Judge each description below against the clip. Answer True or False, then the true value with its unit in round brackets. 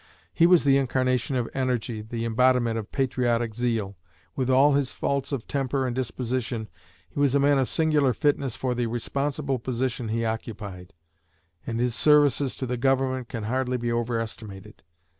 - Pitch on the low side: True (125 Hz)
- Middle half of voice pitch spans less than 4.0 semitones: True (2.6 semitones)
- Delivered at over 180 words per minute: False (165 wpm)